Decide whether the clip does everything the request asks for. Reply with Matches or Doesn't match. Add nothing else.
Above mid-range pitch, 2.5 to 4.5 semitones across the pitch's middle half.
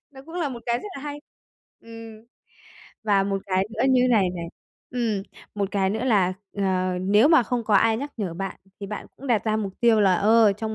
Matches